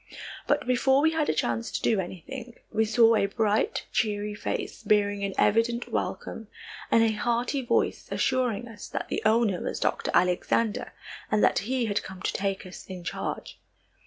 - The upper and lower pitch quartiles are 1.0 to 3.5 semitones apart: Yes, average, 3.0 semitones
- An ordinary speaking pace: Yes, average, 175 wpm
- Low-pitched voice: No, high, 220 Hz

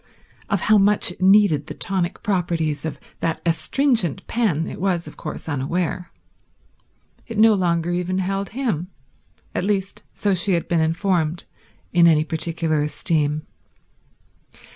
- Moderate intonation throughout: Yes, average, 3.5 semitones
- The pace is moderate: No, slow, 130 wpm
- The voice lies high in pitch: No, medium, 175 Hz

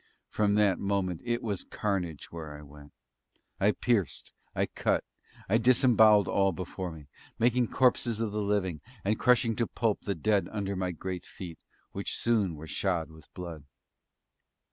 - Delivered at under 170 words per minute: Yes, average, 160 wpm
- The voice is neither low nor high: No, low, 100 Hz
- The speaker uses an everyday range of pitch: Yes, average, 4.2 semitones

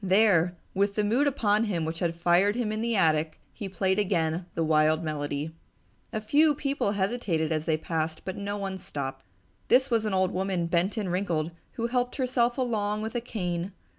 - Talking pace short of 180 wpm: No, average, 195 wpm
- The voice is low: No, high, 190 Hz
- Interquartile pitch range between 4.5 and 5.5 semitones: Yes, average, 5.0 semitones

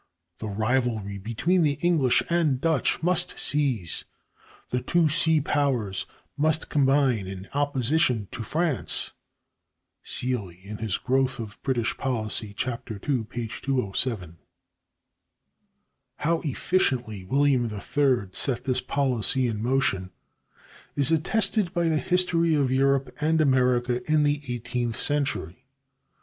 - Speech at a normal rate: No, slow, 110 wpm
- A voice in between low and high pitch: No, low, 130 Hz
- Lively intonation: No, average, 4.5 semitones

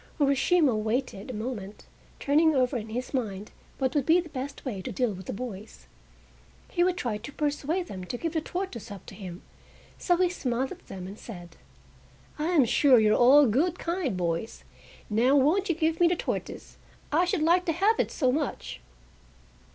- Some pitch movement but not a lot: No, wide, 7.2 semitones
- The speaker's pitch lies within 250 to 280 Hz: Yes, very high, 265 Hz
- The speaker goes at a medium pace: Yes, average, 195 wpm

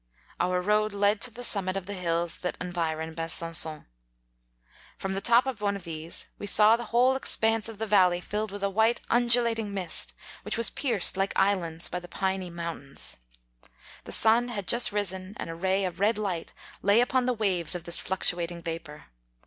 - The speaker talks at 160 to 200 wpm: Yes, average, 195 wpm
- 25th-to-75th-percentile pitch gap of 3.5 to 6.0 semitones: Yes, average, 4.1 semitones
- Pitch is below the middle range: No, high, 195 Hz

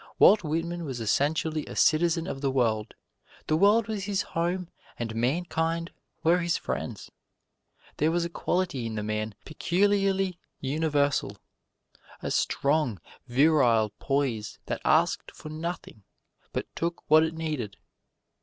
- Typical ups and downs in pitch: Yes, average, 4.8 semitones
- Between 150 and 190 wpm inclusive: No, slow, 135 wpm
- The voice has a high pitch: No, medium, 155 Hz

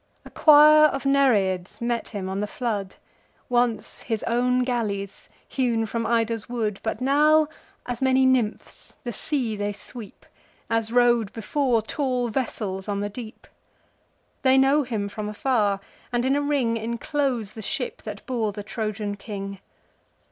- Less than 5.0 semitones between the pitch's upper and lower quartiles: Yes, average, 3.7 semitones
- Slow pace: No, average, 150 wpm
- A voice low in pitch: No, high, 230 Hz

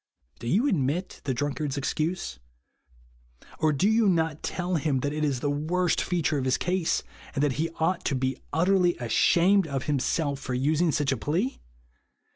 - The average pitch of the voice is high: No, medium, 155 Hz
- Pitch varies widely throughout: No, average, 4.3 semitones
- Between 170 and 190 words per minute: Yes, average, 175 wpm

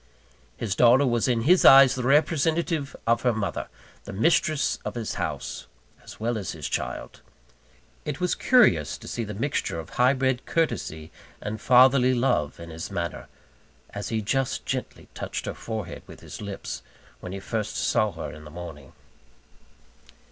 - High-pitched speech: No, low, 120 Hz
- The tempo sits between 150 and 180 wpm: Yes, average, 165 wpm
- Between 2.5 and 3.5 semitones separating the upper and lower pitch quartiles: No, wide, 5.5 semitones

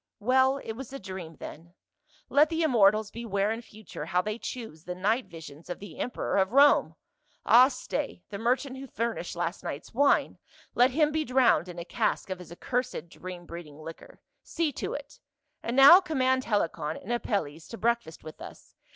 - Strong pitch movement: Yes, wide, 6.8 semitones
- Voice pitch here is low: No, high, 220 Hz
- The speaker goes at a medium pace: Yes, average, 185 wpm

